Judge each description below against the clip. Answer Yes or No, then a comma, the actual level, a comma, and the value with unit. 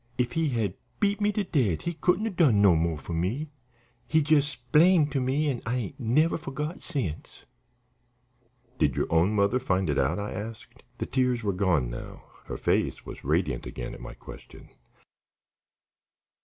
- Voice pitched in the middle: No, low, 125 Hz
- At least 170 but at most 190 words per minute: Yes, average, 175 wpm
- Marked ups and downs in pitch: Yes, wide, 8.8 semitones